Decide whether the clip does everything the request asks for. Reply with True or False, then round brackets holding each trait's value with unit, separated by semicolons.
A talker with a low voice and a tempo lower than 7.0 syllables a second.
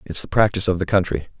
False (90 Hz; 7.5 syllables/s)